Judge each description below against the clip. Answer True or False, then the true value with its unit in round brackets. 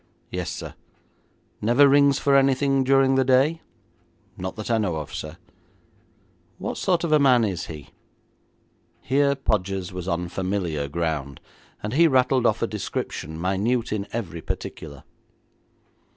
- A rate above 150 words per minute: False (140 wpm)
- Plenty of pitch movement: True (7.5 semitones)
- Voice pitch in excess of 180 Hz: False (110 Hz)